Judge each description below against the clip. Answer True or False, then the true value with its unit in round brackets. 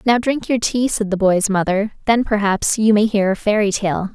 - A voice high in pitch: True (210 Hz)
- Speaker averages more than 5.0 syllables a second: False (4.9 syllables/s)